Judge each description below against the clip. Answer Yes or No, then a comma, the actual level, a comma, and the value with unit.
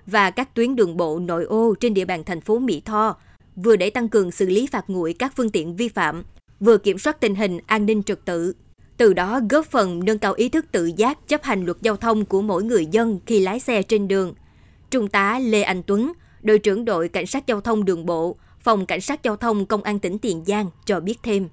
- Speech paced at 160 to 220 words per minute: No, average, 245 wpm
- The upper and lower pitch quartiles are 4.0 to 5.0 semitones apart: No, average, 3.3 semitones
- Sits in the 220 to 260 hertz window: No, high, 210 Hz